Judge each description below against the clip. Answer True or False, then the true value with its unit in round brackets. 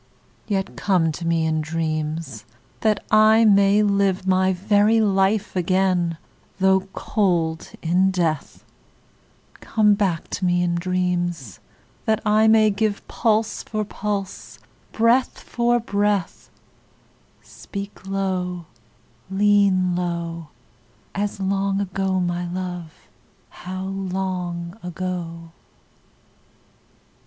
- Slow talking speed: True (100 wpm)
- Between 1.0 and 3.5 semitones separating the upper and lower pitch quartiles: True (2.7 semitones)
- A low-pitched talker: False (190 Hz)